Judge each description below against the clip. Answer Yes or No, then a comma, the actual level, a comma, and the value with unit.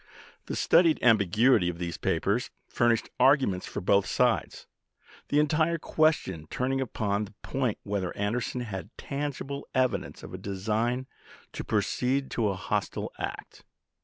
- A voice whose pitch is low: Yes, low, 115 Hz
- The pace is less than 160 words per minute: Yes, slow, 135 wpm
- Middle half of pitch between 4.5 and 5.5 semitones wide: Yes, average, 5.1 semitones